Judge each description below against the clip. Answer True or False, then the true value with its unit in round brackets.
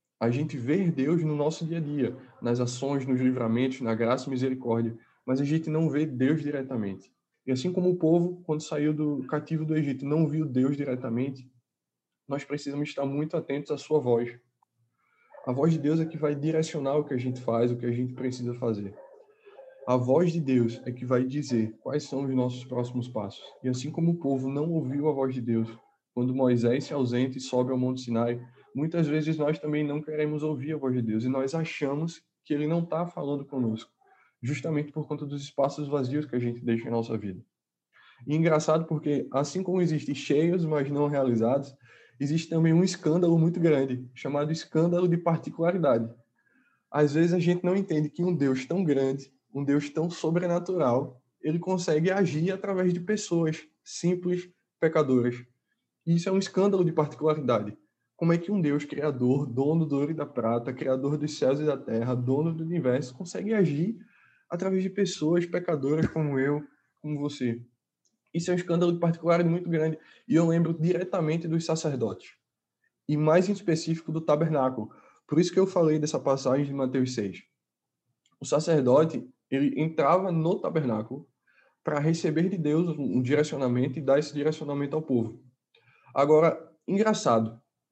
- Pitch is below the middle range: False (150 Hz)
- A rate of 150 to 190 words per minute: True (180 wpm)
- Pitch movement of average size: True (4.2 semitones)